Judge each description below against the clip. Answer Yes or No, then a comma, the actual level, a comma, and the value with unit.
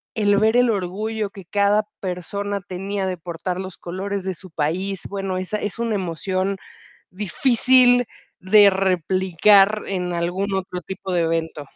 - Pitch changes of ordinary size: No, narrow, 2.1 semitones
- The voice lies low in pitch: No, high, 190 Hz